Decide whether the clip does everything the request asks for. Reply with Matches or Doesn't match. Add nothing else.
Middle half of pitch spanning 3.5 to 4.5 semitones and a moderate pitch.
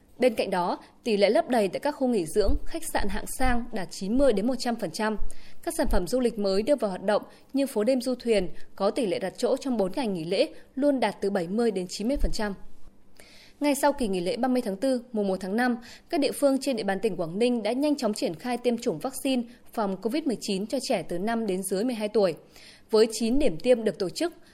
Doesn't match